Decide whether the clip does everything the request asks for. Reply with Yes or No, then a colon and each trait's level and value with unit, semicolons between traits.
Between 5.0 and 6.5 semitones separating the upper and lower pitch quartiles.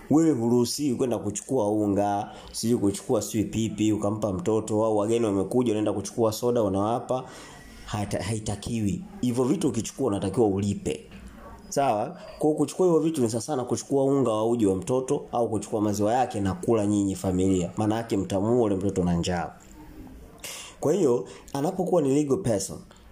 No: average, 3.4 semitones